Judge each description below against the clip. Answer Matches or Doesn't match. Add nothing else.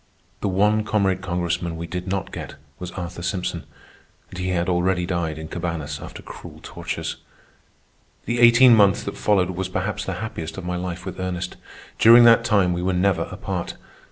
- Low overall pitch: Matches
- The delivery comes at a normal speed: Matches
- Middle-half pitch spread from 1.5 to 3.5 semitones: Matches